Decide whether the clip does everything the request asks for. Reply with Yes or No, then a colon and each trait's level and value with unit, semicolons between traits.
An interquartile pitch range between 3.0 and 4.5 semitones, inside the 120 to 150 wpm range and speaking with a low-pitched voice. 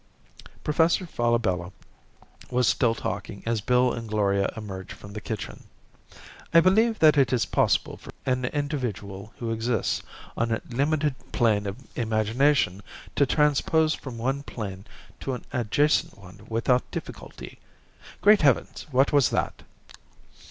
No: average, 5.1 semitones; slow, 135 wpm; low, 120 Hz